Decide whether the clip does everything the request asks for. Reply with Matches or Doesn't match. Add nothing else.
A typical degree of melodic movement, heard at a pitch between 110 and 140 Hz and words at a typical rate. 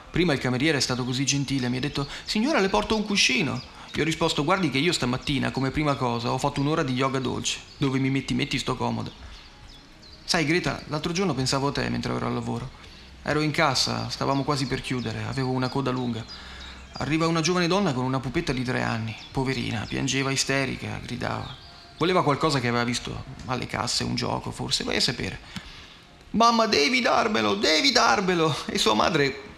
Doesn't match